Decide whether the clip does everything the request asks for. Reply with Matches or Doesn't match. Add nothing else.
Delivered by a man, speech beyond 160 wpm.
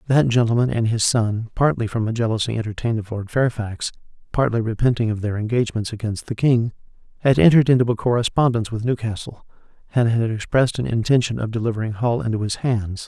Matches